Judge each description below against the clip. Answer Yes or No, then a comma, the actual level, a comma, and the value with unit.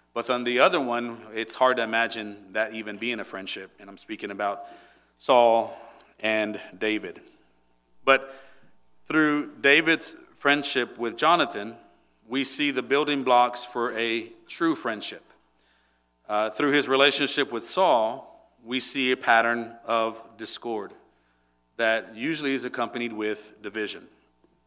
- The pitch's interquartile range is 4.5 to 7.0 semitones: No, average, 3.7 semitones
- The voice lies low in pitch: Yes, low, 115 Hz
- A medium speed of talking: No, slow, 130 wpm